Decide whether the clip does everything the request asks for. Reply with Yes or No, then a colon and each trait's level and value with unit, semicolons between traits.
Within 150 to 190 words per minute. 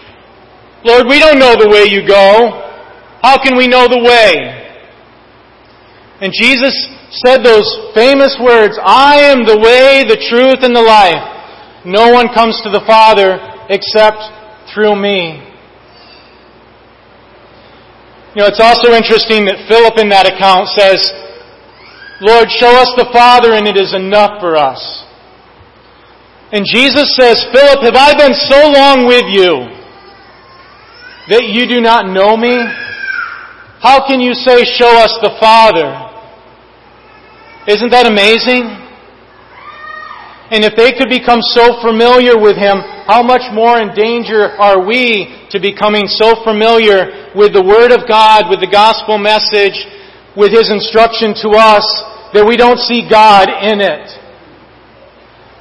No: average, 140 wpm